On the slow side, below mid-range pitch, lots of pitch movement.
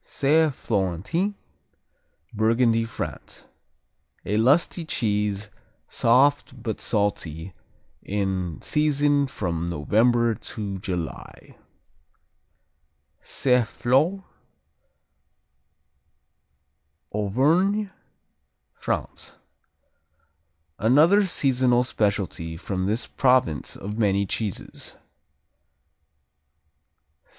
Yes: slow, 65 wpm; low, 115 Hz; wide, 5.7 semitones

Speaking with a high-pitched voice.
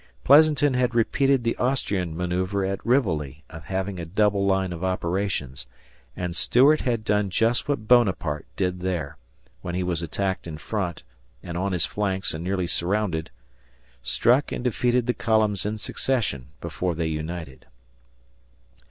No: very low, 95 Hz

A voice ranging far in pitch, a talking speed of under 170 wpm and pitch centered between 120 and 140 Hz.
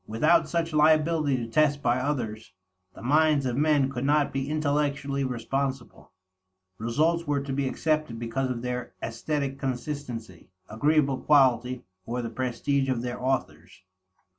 No: average, 3.4 semitones; average, 140 wpm; low, 135 Hz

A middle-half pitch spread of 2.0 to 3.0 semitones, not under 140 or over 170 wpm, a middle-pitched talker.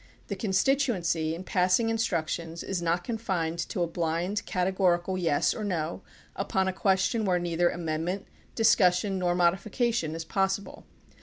Yes: narrow, 2.6 semitones; average, 150 wpm; medium, 180 Hz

